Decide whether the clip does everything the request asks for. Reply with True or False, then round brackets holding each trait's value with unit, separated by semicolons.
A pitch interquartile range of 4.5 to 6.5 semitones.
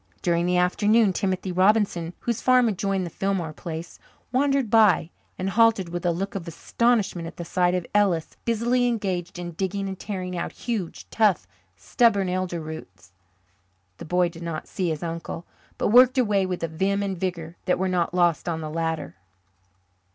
False (3.4 semitones)